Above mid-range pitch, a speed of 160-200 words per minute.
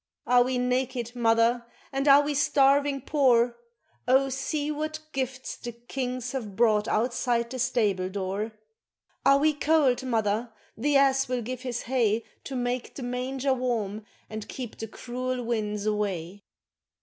No: very high, 250 Hz; average, 150 wpm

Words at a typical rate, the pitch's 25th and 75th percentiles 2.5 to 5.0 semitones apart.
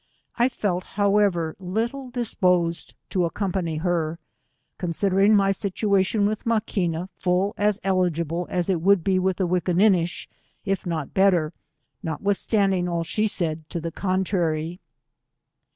No: slow, 125 wpm; average, 2.9 semitones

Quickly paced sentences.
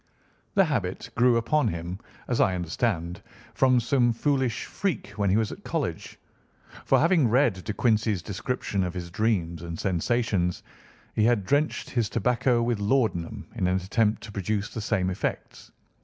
No: average, 160 wpm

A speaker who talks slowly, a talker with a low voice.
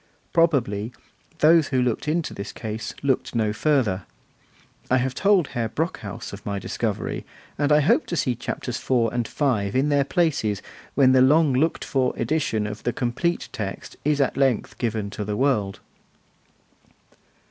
No: average, 160 wpm; low, 130 Hz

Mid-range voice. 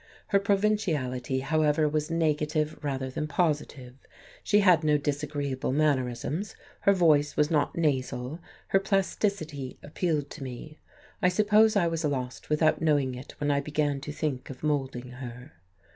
Yes: medium, 150 Hz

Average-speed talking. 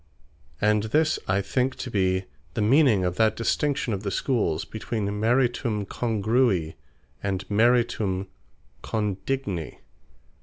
No: slow, 115 wpm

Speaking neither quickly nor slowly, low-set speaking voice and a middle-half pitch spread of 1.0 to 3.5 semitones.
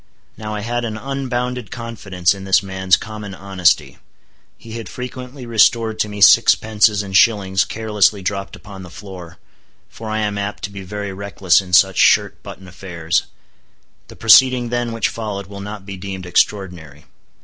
Yes: average, 165 wpm; low, 100 Hz; average, 2.8 semitones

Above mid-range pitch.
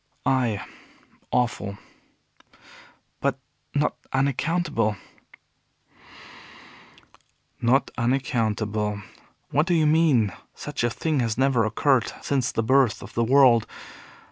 No: low, 125 Hz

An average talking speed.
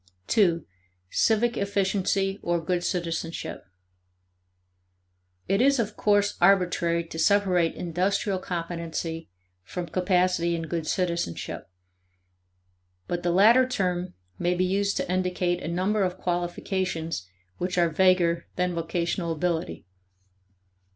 No: slow, 110 wpm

